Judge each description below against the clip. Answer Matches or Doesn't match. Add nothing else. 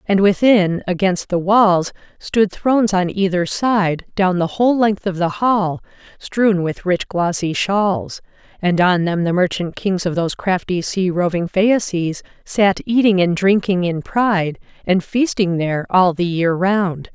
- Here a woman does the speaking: Matches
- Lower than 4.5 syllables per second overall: Matches